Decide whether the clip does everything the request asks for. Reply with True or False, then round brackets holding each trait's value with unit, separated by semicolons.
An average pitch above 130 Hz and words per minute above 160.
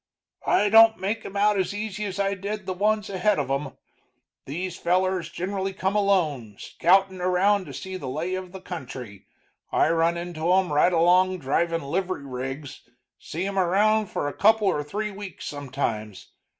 True (185 Hz; 175 wpm)